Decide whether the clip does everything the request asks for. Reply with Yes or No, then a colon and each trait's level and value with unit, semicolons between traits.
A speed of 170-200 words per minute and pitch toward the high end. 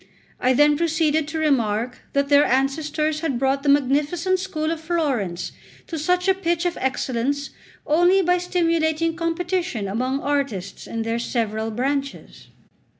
No: average, 145 wpm; very high, 295 Hz